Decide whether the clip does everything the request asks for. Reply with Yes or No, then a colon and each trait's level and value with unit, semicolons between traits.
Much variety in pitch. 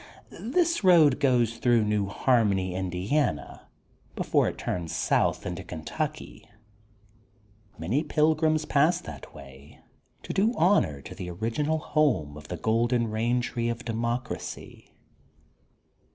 Yes: wide, 8.2 semitones